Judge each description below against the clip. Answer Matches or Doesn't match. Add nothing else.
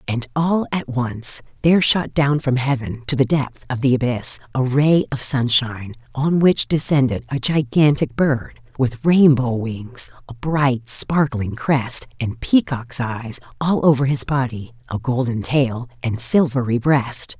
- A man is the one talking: Doesn't match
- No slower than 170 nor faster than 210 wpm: Doesn't match